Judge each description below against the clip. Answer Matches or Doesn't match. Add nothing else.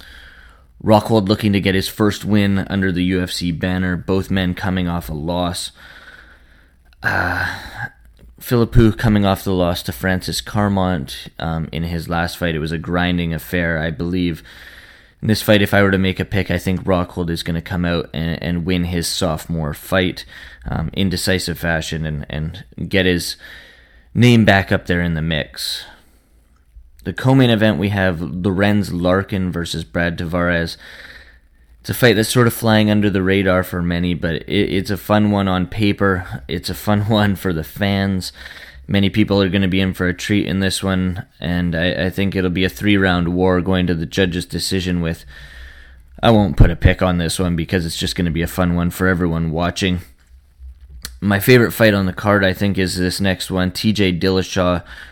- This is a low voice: Matches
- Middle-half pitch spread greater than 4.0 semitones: Doesn't match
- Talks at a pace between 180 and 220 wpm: Matches